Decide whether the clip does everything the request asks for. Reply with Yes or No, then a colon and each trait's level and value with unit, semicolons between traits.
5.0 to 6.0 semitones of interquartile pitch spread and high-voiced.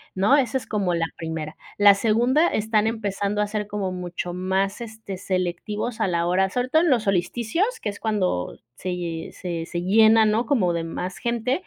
No: average, 3.8 semitones; high, 200 Hz